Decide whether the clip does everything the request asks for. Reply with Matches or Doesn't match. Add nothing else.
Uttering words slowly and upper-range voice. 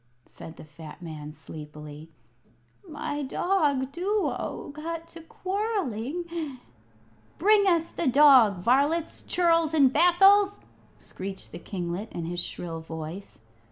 Matches